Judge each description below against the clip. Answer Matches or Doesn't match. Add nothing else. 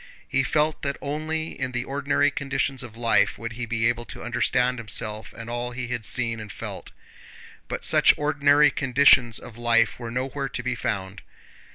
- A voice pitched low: Matches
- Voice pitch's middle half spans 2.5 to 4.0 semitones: Matches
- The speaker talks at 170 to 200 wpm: Matches